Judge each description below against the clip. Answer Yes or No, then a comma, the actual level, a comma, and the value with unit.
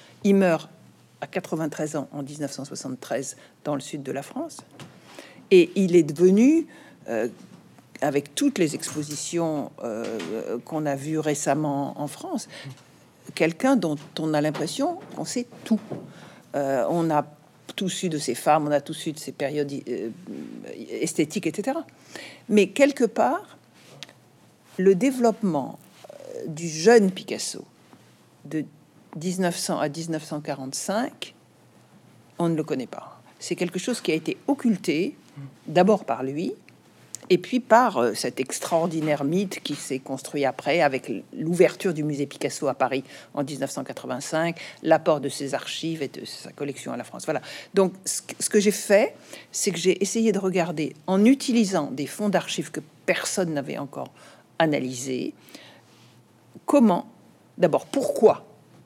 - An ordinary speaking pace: No, slow, 140 wpm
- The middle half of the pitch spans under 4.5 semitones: No, wide, 5.5 semitones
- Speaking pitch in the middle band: Yes, medium, 160 Hz